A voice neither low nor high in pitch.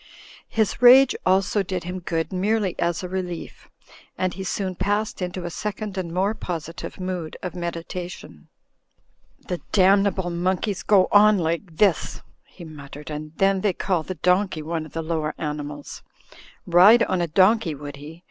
Yes: medium, 180 Hz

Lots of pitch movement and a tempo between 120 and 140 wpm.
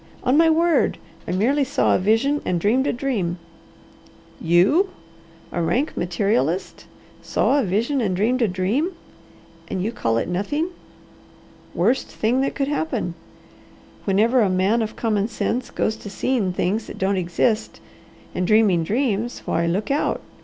No: wide, 6.1 semitones; average, 155 wpm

